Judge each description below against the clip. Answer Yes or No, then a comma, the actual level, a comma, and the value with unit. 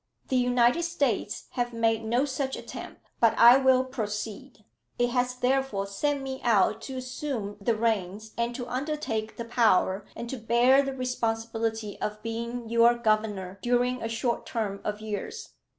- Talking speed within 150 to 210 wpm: Yes, average, 160 wpm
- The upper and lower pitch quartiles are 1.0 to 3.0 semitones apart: Yes, average, 2.7 semitones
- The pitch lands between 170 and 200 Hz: No, high, 235 Hz